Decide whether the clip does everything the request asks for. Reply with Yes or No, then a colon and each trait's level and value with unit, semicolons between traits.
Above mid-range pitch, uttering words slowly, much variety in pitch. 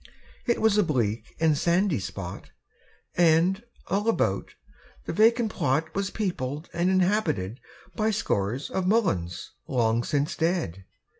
No: medium, 165 Hz; slow, 130 wpm; wide, 8.3 semitones